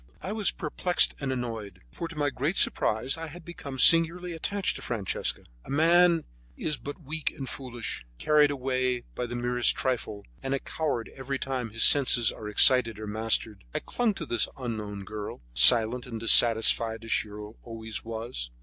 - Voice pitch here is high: No, low, 125 Hz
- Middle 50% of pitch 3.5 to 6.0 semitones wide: Yes, average, 5.1 semitones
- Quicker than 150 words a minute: Yes, average, 175 wpm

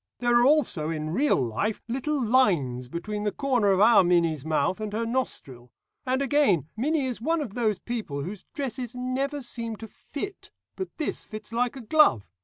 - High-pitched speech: Yes, high, 230 Hz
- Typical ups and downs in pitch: No, wide, 6.8 semitones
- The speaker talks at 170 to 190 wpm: Yes, average, 185 wpm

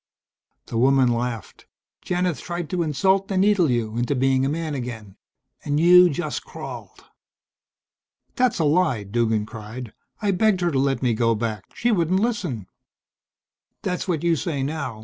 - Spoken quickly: No, average, 160 wpm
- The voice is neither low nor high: Yes, medium, 145 Hz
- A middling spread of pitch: No, wide, 7.0 semitones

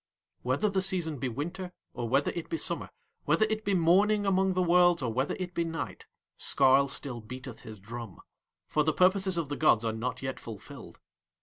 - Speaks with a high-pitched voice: No, medium, 155 Hz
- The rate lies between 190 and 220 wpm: Yes, average, 195 wpm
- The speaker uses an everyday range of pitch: No, wide, 6.4 semitones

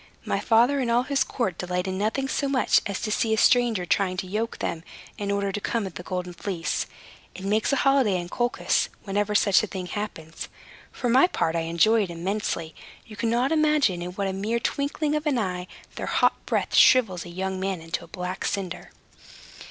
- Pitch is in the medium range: No, high, 200 Hz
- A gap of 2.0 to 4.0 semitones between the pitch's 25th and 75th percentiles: No, average, 4.7 semitones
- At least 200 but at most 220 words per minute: Yes, fast, 205 wpm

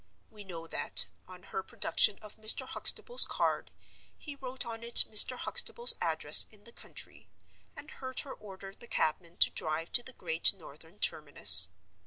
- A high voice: Yes, high, 210 Hz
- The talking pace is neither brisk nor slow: Yes, average, 165 wpm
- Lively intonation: Yes, wide, 6.9 semitones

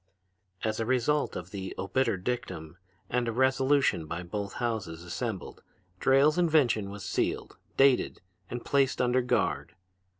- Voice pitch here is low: Yes, low, 120 Hz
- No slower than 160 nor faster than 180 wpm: No, slow, 135 wpm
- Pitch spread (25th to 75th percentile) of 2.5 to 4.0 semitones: No, average, 5.3 semitones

